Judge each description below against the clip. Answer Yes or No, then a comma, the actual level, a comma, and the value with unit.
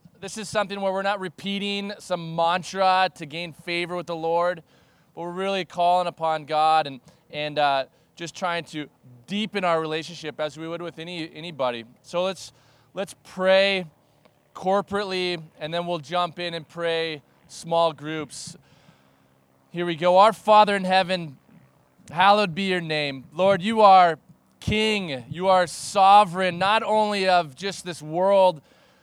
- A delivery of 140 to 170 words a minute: Yes, average, 155 wpm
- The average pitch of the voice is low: No, medium, 175 Hz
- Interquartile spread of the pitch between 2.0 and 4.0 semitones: Yes, average, 3.4 semitones